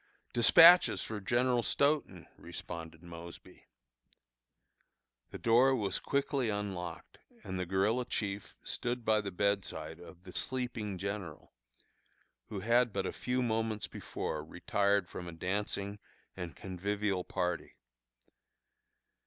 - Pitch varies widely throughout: No, average, 4.6 semitones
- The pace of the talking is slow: Yes, slow, 115 wpm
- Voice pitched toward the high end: No, low, 100 Hz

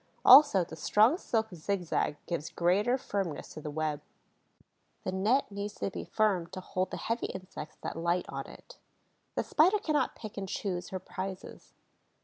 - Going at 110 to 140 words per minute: No, average, 165 wpm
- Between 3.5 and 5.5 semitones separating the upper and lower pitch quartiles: Yes, average, 4.0 semitones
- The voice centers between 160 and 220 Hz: Yes, high, 190 Hz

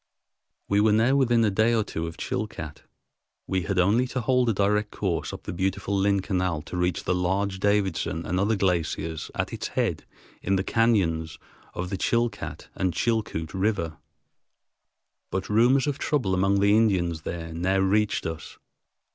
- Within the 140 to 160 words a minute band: No, average, 170 wpm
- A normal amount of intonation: Yes, average, 3.6 semitones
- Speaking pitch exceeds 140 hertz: No, very low, 95 Hz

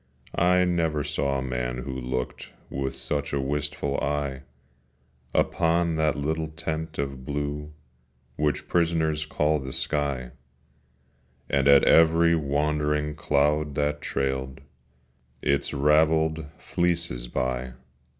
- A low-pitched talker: Yes, very low, 75 Hz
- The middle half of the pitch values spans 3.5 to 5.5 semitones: No, narrow, 2.5 semitones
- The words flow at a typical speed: No, slow, 110 wpm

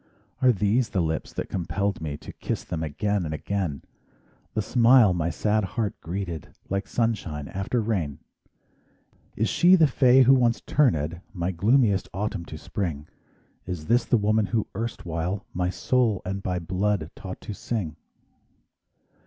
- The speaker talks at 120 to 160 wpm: Yes, average, 155 wpm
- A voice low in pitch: Yes, low, 100 Hz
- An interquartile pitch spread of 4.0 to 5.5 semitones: Yes, average, 5.0 semitones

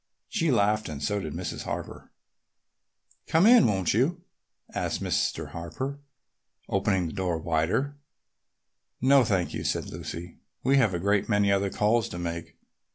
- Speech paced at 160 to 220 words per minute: No, average, 150 wpm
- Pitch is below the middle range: Yes, low, 100 Hz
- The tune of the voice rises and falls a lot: Yes, wide, 7.0 semitones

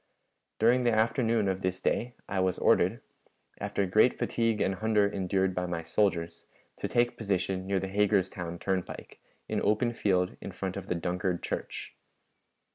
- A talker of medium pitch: No, very low, 95 Hz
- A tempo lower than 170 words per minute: Yes, average, 160 wpm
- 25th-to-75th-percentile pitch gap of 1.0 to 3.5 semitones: Yes, average, 2.9 semitones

